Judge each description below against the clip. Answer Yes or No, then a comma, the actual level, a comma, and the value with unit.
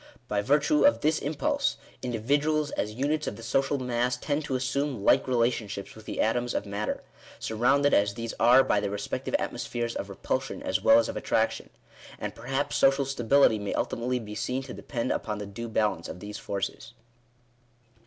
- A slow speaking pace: No, average, 185 wpm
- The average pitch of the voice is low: Yes, low, 120 Hz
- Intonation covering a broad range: No, average, 4.6 semitones